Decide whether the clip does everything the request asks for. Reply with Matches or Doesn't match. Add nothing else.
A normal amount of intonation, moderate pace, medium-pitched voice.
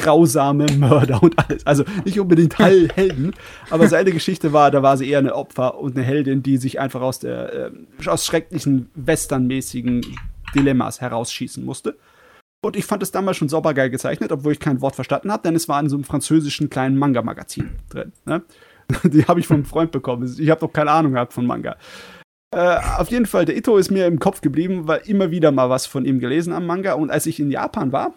Doesn't match